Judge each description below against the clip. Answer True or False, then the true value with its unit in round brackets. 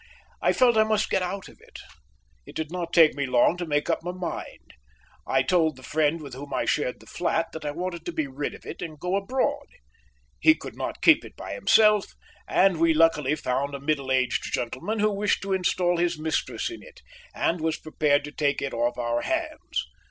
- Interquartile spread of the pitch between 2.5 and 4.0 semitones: False (4.5 semitones)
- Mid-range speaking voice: True (160 Hz)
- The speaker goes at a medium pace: False (215 wpm)